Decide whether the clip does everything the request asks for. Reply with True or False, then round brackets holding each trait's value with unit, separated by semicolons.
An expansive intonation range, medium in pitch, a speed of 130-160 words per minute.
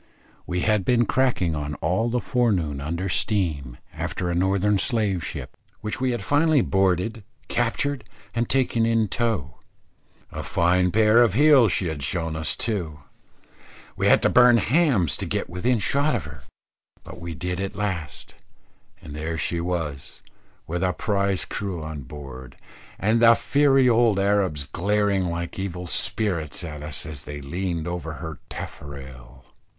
False (6.1 semitones; 95 Hz; 155 wpm)